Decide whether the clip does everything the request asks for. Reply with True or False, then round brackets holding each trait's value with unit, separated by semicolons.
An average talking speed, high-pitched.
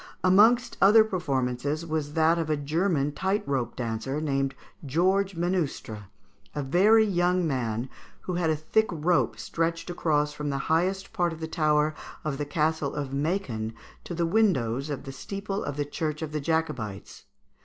False (165 wpm; 155 Hz)